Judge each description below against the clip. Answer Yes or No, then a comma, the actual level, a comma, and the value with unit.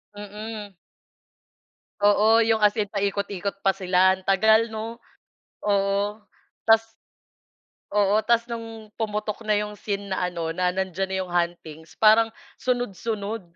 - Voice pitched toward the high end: Yes, high, 205 Hz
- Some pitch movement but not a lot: No, narrow, 2.3 semitones